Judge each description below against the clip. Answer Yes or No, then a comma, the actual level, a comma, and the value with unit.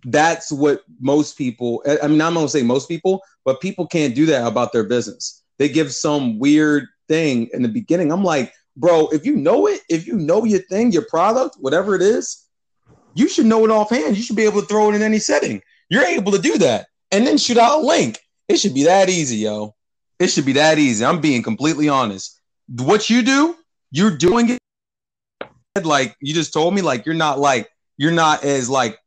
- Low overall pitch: No, medium, 160 Hz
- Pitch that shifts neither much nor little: No, wide, 7.2 semitones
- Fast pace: Yes, fast, 215 wpm